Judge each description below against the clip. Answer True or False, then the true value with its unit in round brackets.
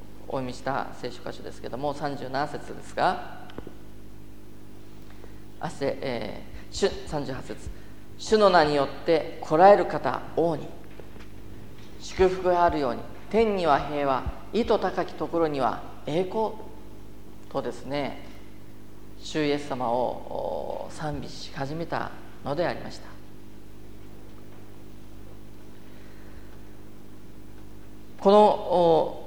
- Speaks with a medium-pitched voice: False (110 Hz)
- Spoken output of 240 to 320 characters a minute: False (180 characters per minute)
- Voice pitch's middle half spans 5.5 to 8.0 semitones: True (7.4 semitones)